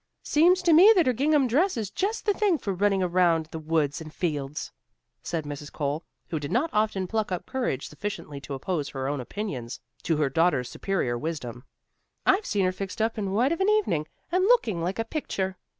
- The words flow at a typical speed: No, fast, 210 wpm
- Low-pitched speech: No, medium, 185 Hz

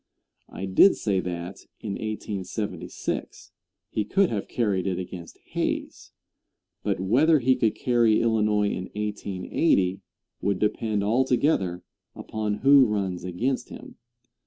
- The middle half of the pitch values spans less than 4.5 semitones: Yes, average, 3.8 semitones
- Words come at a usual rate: No, slow, 120 wpm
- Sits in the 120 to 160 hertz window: No, low, 105 Hz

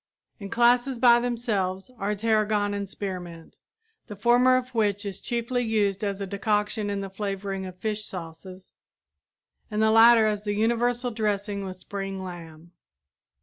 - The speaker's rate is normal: Yes, average, 150 wpm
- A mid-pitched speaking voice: No, high, 205 Hz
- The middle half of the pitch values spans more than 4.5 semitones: No, average, 2.8 semitones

